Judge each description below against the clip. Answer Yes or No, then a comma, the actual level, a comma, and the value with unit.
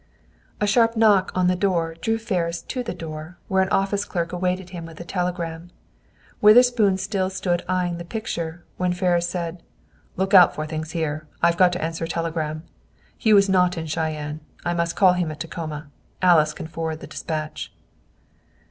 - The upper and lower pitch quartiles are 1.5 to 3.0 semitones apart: Yes, narrow, 2.5 semitones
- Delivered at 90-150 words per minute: No, average, 180 wpm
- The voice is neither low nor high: Yes, medium, 175 Hz